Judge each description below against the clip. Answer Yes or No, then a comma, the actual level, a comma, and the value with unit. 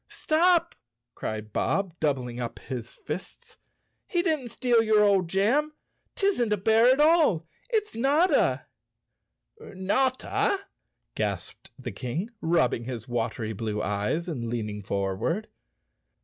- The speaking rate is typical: No, slow, 130 wpm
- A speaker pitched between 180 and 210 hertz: Yes, medium, 185 Hz